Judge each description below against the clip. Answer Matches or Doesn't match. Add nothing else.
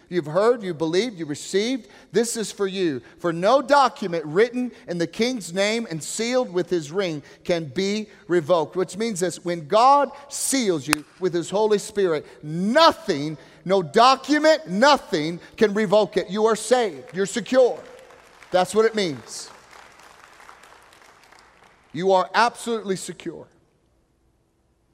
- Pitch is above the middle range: Matches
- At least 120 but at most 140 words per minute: Matches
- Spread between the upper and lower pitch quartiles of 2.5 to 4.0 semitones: Doesn't match